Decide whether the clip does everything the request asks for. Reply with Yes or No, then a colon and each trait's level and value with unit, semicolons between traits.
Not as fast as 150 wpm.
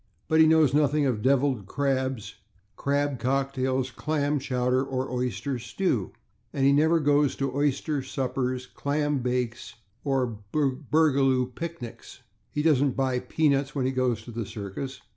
Yes: average, 140 wpm